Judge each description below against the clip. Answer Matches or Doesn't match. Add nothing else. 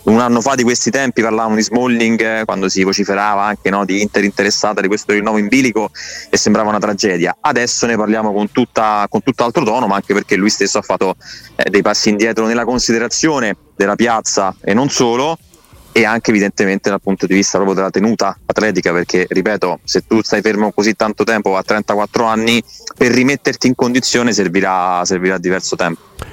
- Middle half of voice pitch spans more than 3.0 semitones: Doesn't match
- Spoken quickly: Matches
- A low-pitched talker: Matches